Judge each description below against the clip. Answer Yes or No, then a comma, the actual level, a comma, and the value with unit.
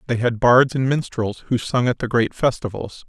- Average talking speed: No, fast, 215 wpm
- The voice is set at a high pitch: No, low, 120 Hz